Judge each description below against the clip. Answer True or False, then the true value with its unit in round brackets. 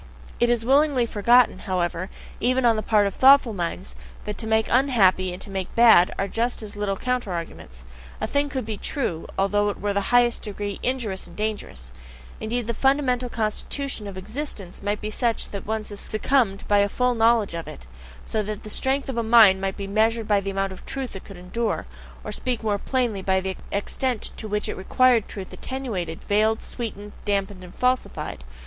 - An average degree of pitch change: True (3.6 semitones)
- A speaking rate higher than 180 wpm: True (200 wpm)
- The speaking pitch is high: True (215 Hz)